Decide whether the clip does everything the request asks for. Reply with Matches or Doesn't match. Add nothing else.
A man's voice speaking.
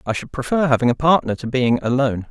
Matches